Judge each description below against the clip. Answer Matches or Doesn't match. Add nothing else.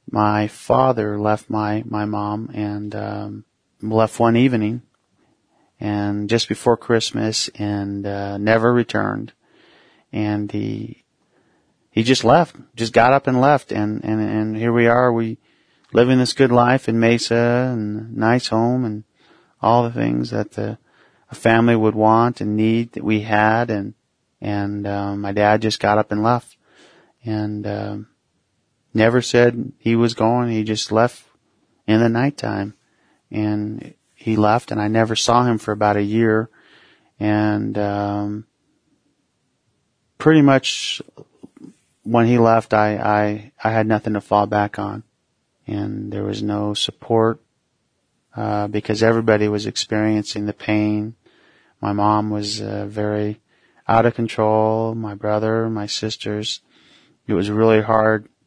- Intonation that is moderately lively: Doesn't match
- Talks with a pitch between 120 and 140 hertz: Doesn't match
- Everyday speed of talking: Matches